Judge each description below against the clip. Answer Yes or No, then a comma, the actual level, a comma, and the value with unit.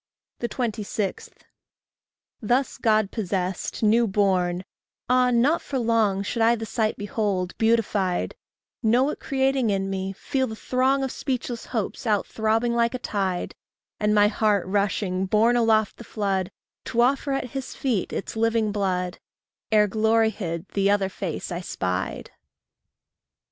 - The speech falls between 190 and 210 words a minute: No, average, 145 wpm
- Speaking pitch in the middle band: No, high, 215 Hz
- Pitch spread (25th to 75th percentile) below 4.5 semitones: Yes, average, 3.5 semitones